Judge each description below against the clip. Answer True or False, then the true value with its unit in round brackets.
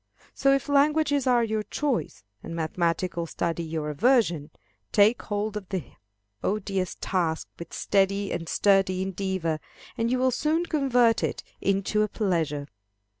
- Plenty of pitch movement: True (6.1 semitones)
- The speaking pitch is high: True (200 Hz)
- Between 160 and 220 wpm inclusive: False (140 wpm)